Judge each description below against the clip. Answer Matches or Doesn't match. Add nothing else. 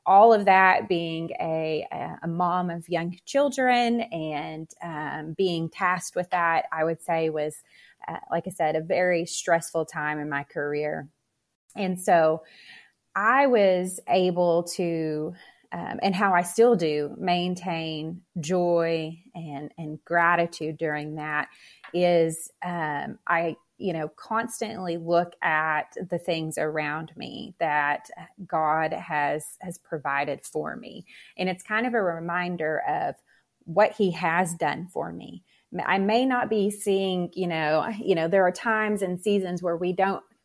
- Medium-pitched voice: Matches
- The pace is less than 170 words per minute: Matches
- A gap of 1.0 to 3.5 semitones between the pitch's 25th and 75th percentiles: Matches